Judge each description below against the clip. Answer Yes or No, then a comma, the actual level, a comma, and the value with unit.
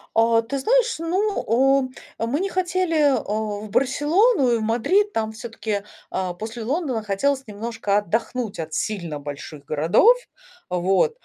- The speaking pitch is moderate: No, high, 230 Hz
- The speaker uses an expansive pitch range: Yes, wide, 6.8 semitones